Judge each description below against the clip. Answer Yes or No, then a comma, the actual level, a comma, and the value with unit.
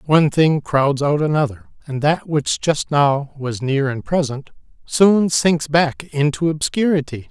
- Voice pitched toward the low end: No, medium, 150 Hz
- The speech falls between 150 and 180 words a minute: Yes, average, 155 wpm